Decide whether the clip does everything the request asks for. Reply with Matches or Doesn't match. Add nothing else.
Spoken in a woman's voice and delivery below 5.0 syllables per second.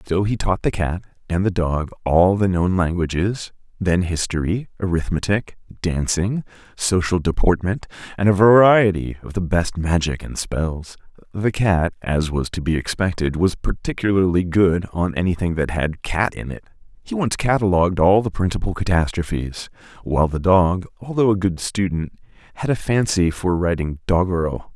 Doesn't match